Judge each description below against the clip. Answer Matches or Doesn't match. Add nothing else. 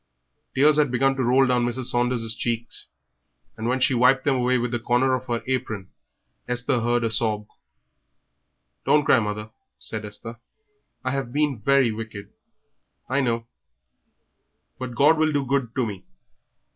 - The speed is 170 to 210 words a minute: Doesn't match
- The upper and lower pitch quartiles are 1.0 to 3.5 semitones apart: Matches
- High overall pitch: Doesn't match